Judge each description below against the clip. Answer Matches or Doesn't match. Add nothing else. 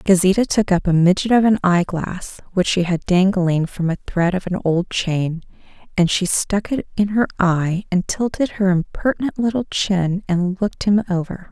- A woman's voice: Matches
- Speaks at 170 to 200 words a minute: Matches